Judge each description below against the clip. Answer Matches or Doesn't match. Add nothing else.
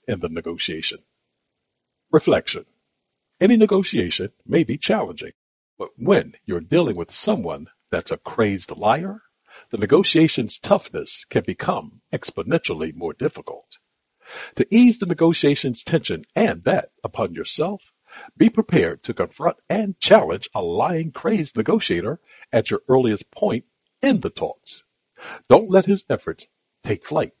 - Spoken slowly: Matches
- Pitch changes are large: Matches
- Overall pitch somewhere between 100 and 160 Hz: Doesn't match